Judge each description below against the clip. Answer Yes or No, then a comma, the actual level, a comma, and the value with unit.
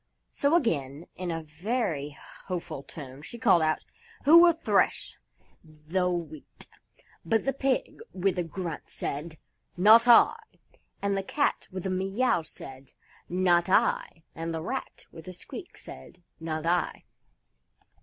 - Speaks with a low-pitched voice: No, medium, 175 Hz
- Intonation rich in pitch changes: No, average, 4.2 semitones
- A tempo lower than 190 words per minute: Yes, average, 140 wpm